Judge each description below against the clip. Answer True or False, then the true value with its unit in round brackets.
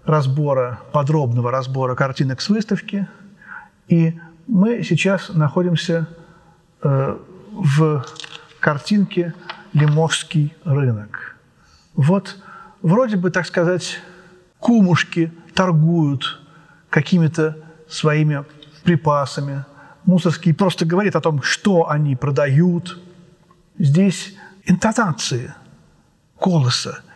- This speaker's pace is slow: True (80 wpm)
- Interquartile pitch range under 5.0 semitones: True (3.4 semitones)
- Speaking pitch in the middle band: True (165 Hz)